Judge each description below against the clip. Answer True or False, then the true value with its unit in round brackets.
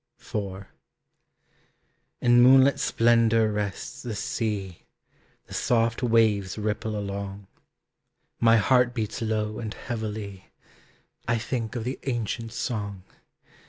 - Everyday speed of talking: False (105 wpm)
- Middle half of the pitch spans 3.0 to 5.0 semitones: False (2.4 semitones)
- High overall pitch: False (110 Hz)